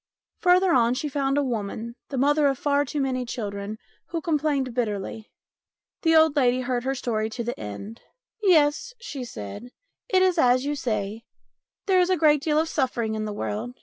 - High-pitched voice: Yes, very high, 260 Hz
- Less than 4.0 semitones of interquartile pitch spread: No, average, 4.8 semitones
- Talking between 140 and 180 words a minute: No, average, 195 wpm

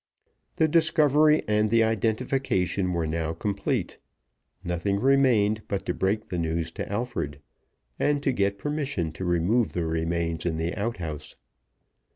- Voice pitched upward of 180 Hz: No, low, 100 Hz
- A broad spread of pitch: Yes, wide, 6.6 semitones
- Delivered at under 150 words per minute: Yes, average, 140 wpm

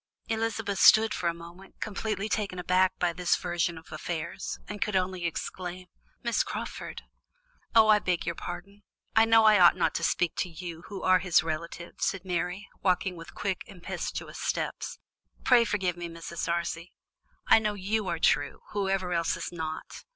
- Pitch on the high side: No, medium, 180 Hz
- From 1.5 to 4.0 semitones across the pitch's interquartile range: Yes, average, 3.0 semitones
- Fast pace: No, average, 180 wpm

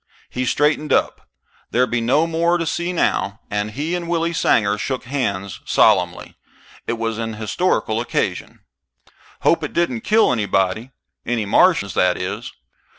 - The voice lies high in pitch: No, low, 120 Hz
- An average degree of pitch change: No, wide, 7.6 semitones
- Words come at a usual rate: Yes, average, 150 wpm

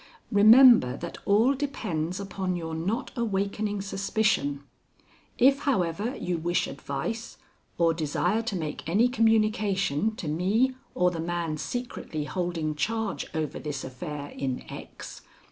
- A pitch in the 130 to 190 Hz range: Yes, medium, 185 Hz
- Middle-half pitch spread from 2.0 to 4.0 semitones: No, wide, 5.6 semitones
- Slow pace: Yes, slow, 130 wpm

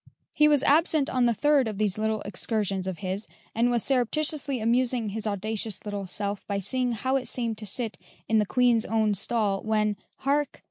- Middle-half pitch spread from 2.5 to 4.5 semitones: Yes, average, 3.7 semitones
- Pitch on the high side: Yes, high, 220 Hz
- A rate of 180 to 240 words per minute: Yes, average, 190 wpm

